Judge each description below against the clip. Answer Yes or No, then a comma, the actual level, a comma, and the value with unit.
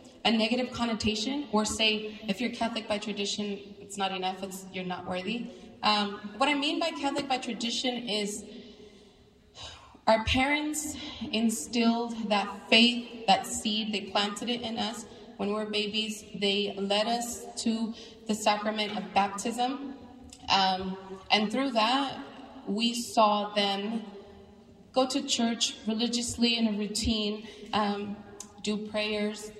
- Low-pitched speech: No, high, 215 Hz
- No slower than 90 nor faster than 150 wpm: Yes, slow, 135 wpm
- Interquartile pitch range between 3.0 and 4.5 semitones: No, narrow, 2.4 semitones